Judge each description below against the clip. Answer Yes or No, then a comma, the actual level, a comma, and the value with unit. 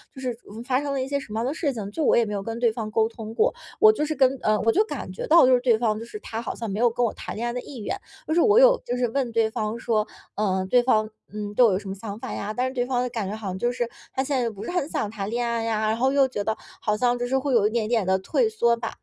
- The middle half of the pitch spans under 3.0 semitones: No, average, 3.4 semitones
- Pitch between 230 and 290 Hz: Yes, high, 235 Hz